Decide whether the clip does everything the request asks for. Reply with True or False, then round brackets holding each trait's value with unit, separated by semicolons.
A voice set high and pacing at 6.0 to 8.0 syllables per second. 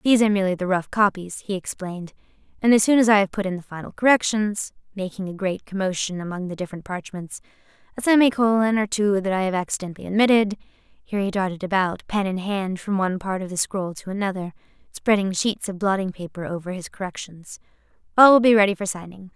True (195 Hz; 6.3 syllables/s)